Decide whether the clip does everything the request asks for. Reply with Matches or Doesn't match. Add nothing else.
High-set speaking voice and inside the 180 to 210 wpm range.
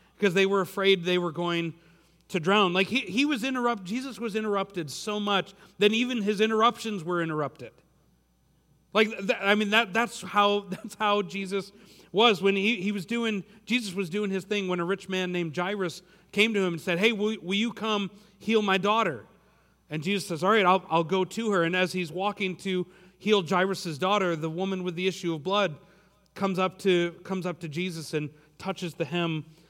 Matches